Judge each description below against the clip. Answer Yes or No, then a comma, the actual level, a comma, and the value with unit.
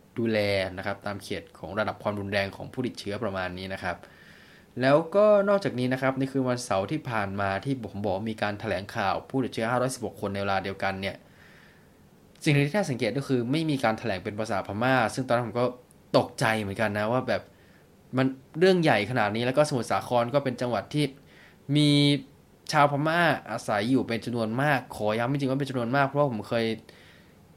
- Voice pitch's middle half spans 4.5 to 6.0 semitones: Yes, average, 4.9 semitones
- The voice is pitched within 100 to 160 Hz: Yes, low, 120 Hz